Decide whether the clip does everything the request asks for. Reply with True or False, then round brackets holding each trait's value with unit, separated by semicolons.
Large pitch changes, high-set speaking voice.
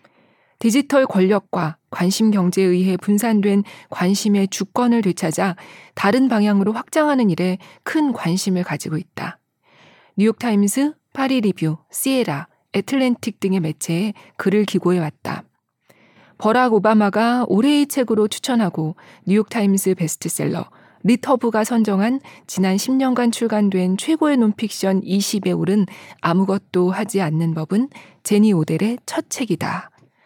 False (4.0 semitones; 205 Hz)